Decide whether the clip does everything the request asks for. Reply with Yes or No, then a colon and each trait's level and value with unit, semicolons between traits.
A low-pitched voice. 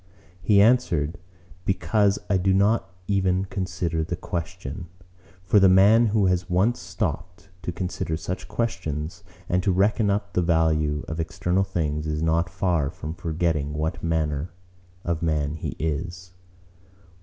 Yes: very low, 90 Hz